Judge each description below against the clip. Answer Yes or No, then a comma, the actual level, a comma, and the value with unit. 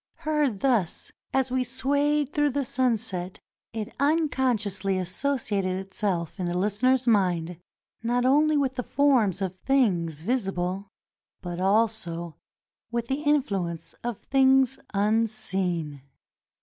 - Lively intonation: Yes, wide, 6.1 semitones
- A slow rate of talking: Yes, slow, 115 wpm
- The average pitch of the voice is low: No, high, 225 Hz